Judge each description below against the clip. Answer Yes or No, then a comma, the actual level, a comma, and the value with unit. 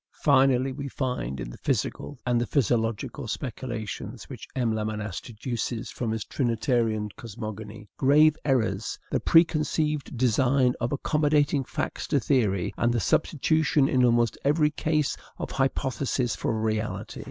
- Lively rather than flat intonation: No, average, 4.3 semitones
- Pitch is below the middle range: Yes, low, 125 Hz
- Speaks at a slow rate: Yes, slow, 130 wpm